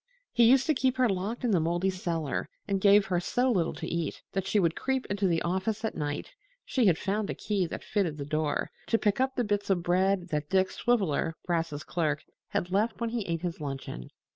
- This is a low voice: No, high, 190 Hz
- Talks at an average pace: No, fast, 225 wpm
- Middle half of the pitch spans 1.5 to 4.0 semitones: No, average, 4.6 semitones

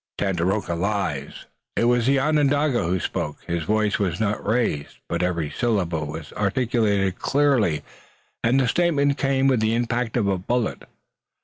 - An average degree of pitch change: No, wide, 6.0 semitones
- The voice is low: Yes, low, 110 Hz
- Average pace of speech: Yes, average, 150 wpm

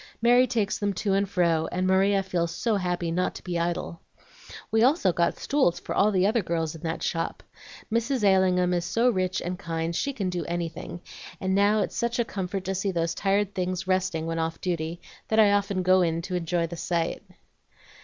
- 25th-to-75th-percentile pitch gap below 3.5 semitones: Yes, average, 2.9 semitones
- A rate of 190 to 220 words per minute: Yes, fast, 205 wpm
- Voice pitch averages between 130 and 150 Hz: No, medium, 185 Hz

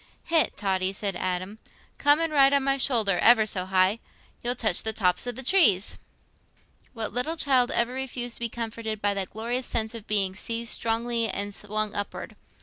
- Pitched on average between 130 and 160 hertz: No, high, 225 Hz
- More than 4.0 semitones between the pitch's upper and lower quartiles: No, average, 3.5 semitones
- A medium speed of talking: Yes, average, 175 wpm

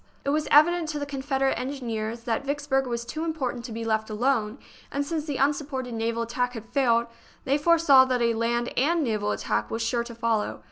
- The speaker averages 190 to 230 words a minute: Yes, average, 200 wpm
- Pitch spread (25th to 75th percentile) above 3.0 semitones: Yes, average, 3.7 semitones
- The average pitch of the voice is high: Yes, very high, 255 Hz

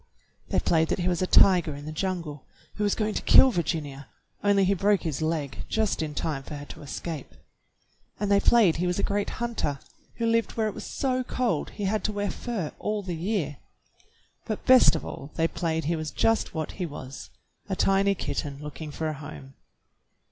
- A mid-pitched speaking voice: Yes, medium, 175 Hz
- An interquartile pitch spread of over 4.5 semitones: Yes, average, 5.2 semitones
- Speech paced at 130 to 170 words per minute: No, fast, 205 wpm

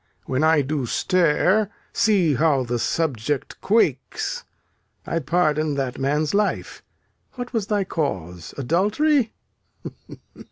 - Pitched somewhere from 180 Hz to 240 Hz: No, medium, 155 Hz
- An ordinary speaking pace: No, slow, 110 wpm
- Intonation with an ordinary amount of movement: No, wide, 6.7 semitones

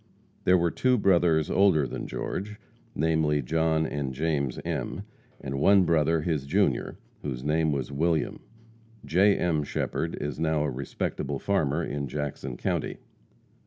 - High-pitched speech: No, very low, 80 Hz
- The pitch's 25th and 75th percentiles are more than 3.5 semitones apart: No, average, 2.9 semitones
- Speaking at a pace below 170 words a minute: Yes, average, 140 wpm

